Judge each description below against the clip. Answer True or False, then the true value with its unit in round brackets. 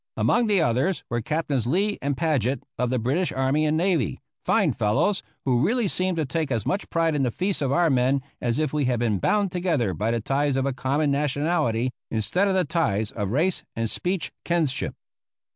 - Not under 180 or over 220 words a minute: True (205 wpm)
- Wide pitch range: True (5.7 semitones)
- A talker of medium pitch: True (145 Hz)